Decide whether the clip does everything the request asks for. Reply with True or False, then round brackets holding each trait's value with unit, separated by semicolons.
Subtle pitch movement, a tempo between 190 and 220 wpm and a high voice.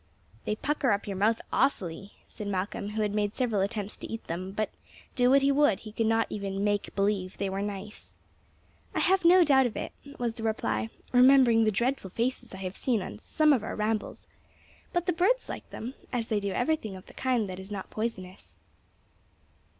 False (4.2 semitones; 205 wpm; 215 Hz)